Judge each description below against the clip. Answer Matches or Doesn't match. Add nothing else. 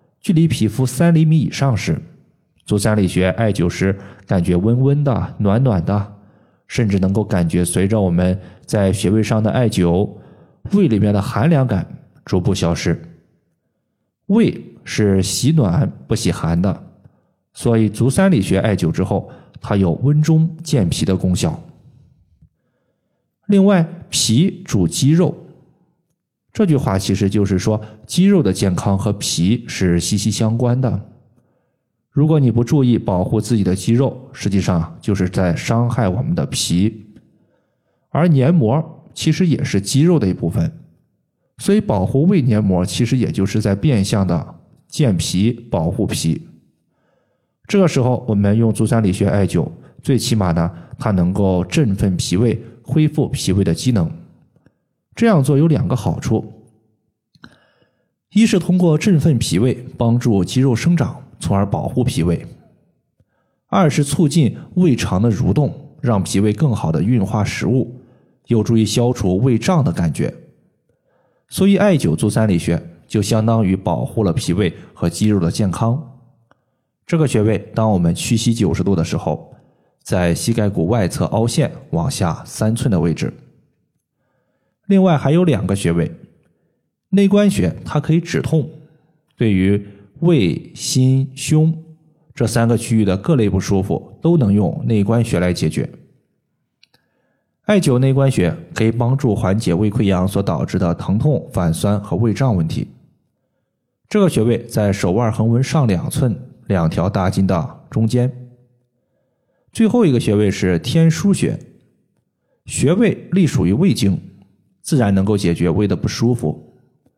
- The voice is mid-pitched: Doesn't match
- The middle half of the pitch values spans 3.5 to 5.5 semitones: Doesn't match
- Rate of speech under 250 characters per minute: Matches